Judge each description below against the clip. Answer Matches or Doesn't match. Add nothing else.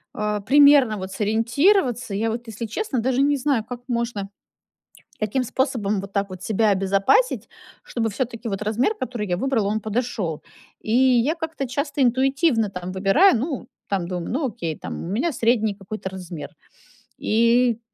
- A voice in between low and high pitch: Doesn't match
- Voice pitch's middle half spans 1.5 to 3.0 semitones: Doesn't match